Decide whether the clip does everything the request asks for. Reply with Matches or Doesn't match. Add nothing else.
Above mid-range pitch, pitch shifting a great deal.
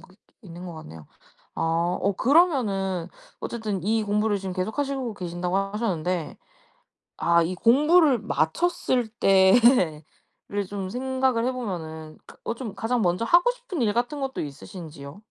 Matches